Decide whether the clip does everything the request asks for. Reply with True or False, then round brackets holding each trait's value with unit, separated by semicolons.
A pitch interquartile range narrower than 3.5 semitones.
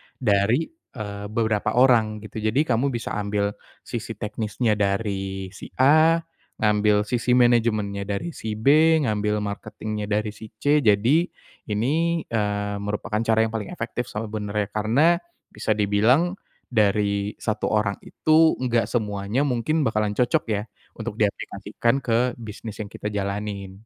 True (3.0 semitones)